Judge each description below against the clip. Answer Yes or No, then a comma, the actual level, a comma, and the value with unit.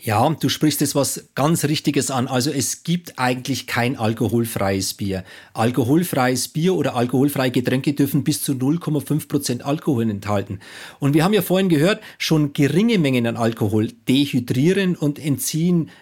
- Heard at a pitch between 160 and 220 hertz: No, medium, 140 Hz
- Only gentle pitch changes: No, average, 3.9 semitones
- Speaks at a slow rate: No, average, 150 wpm